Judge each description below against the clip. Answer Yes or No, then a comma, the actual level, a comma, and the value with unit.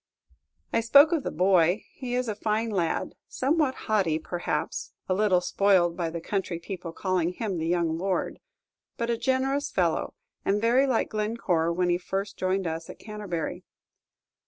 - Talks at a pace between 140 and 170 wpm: Yes, average, 165 wpm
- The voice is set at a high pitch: Yes, high, 195 Hz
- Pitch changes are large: No, average, 4.8 semitones